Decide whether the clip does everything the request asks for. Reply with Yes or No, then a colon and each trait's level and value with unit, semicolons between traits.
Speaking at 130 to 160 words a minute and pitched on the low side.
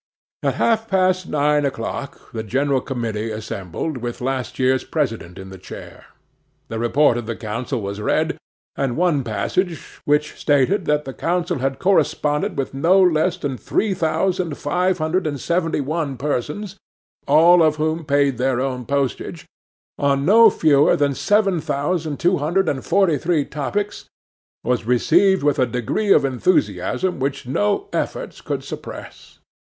No: average, 155 wpm; medium, 145 Hz